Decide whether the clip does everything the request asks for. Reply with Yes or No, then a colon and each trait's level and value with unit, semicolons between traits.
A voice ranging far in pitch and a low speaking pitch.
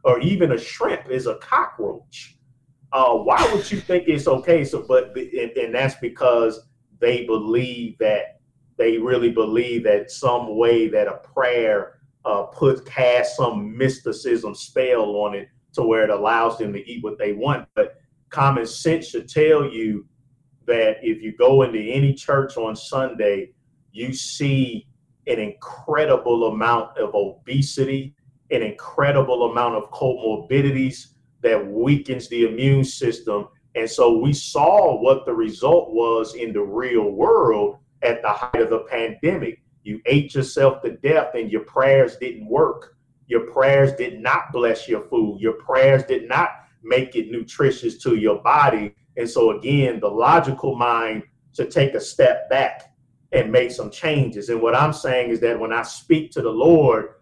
Yes: wide, 5.8 semitones; low, 130 Hz